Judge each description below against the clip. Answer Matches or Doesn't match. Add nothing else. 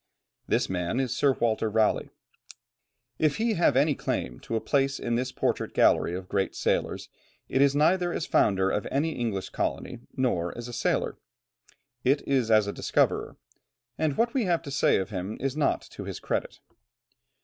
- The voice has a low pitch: Matches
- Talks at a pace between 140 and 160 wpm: Doesn't match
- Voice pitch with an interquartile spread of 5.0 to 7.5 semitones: Matches